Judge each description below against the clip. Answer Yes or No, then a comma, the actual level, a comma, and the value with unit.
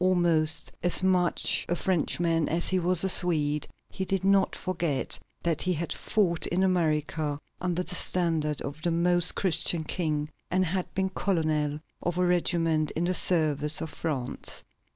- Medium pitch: Yes, medium, 170 Hz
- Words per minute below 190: Yes, average, 160 wpm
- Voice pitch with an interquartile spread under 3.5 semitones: Yes, average, 2.7 semitones